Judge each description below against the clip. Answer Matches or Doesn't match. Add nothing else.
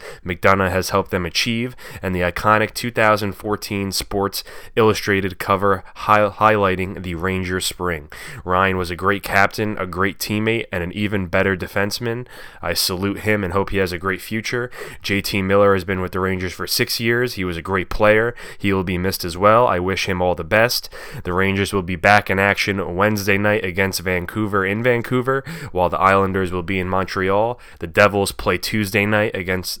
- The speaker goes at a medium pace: Matches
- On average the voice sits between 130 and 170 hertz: Doesn't match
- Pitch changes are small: Matches